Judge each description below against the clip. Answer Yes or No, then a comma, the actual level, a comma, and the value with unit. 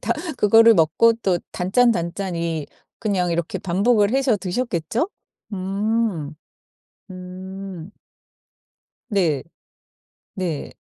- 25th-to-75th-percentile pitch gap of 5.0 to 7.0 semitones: No, average, 4.4 semitones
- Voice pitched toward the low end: No, high, 190 Hz